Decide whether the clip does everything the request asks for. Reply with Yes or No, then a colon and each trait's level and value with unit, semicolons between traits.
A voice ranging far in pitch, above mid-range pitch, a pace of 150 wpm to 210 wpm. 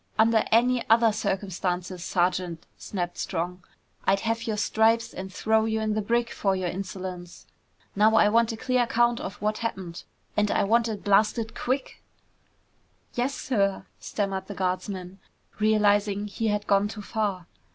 No: average, 3.0 semitones; high, 210 Hz; average, 155 wpm